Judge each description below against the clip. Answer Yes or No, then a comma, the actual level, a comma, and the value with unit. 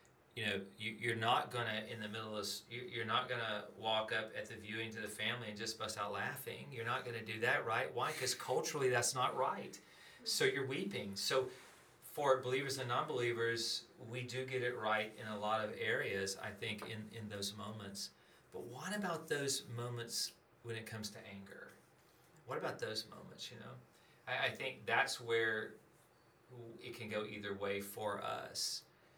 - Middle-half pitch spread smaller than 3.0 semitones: Yes, narrow, 2.4 semitones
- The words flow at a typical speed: Yes, average, 185 wpm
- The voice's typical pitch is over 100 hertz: Yes, low, 110 Hz